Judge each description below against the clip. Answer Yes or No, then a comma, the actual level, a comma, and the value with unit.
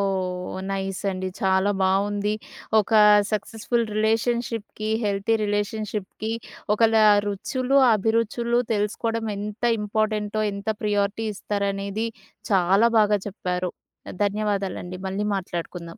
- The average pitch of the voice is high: Yes, high, 205 Hz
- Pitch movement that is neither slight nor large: No, narrow, 2.0 semitones